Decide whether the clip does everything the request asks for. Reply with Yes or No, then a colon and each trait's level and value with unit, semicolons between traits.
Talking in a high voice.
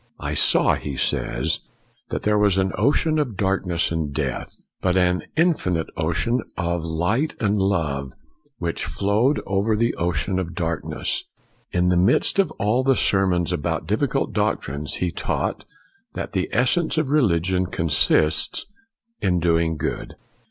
No: very low, 90 Hz